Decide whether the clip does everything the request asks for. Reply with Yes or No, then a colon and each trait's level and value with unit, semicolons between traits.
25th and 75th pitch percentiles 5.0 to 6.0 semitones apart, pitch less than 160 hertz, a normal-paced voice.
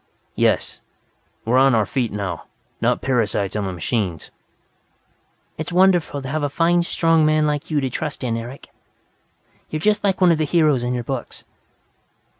Yes: wide, 5.5 semitones; medium, 140 Hz; average, 170 wpm